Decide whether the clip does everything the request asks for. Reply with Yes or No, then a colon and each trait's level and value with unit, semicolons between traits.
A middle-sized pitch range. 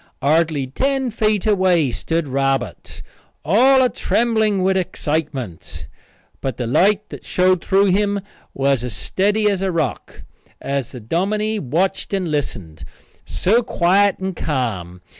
No: wide, 7.0 semitones